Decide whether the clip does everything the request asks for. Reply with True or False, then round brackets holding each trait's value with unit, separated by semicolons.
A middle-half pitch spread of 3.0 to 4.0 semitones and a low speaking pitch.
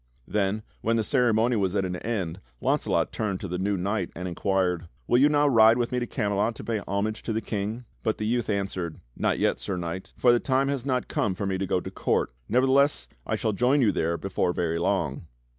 False (4.4 semitones; 105 Hz)